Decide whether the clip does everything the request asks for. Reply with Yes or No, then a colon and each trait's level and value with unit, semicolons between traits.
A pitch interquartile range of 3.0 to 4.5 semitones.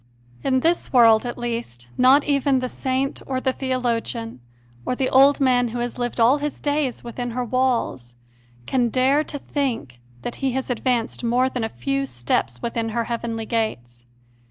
No: narrow, 2.5 semitones